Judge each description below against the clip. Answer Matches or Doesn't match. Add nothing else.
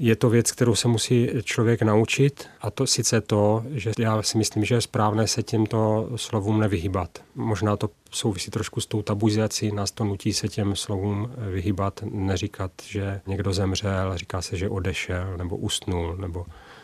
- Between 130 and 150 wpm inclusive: Doesn't match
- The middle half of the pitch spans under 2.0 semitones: Doesn't match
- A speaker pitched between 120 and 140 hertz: Doesn't match